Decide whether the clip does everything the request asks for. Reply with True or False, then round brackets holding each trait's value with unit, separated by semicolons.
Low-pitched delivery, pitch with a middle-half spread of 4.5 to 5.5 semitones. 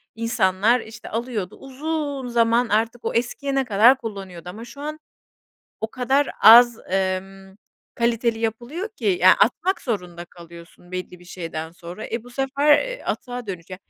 False (230 Hz; 5.1 semitones)